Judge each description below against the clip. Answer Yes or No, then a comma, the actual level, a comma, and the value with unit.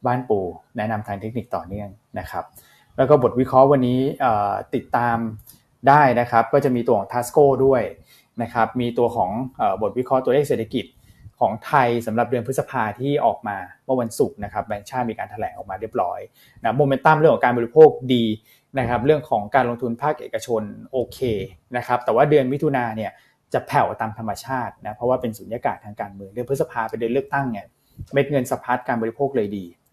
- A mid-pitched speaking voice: No, low, 120 Hz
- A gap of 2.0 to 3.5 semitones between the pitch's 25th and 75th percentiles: Yes, average, 3.1 semitones